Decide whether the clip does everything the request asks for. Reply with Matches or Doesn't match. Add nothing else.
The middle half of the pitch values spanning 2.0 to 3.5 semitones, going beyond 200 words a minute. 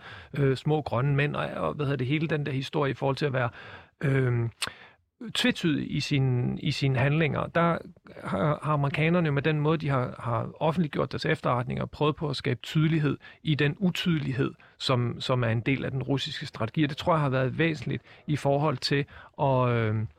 Doesn't match